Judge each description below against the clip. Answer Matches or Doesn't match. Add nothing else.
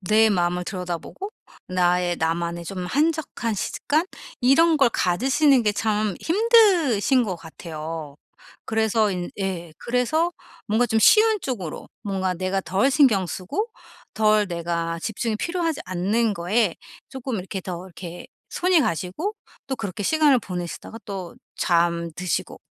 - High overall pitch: Matches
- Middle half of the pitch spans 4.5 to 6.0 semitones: Doesn't match